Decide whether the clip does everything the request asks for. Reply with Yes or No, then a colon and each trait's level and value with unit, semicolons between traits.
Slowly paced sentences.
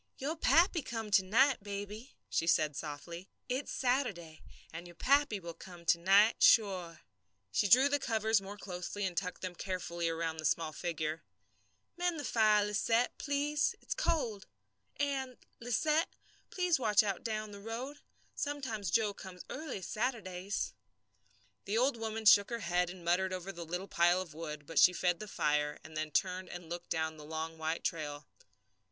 No: average, 170 wpm